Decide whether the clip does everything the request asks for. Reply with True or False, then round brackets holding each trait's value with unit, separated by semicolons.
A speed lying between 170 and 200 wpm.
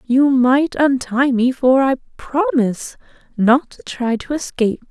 False (145 wpm)